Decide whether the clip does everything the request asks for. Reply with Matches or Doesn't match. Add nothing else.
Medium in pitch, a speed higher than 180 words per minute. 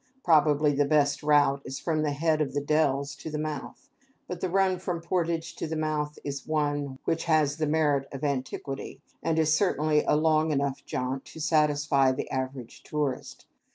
Matches